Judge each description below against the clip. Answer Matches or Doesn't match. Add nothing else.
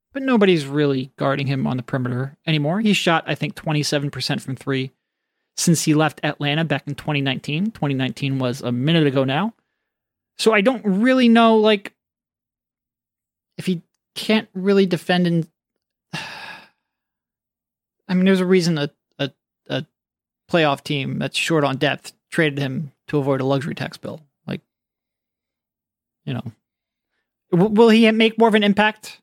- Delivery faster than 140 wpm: Matches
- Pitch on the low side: Doesn't match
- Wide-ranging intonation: Matches